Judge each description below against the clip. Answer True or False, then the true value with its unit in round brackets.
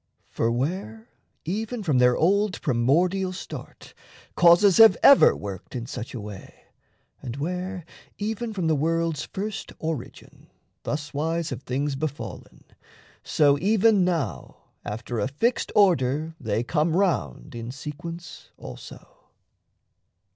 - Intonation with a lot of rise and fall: True (6.7 semitones)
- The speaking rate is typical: False (120 wpm)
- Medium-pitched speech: True (155 Hz)